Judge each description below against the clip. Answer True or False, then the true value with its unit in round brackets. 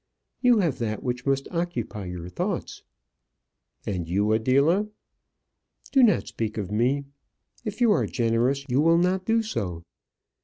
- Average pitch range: False (8.5 semitones)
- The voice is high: False (130 Hz)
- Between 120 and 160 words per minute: True (150 wpm)